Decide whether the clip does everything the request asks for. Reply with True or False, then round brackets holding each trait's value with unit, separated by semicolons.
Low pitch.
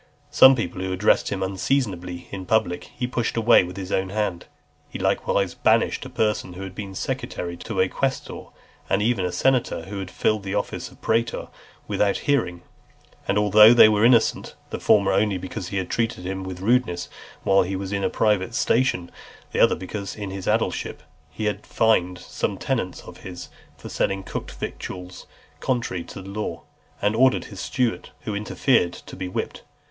True (100 Hz)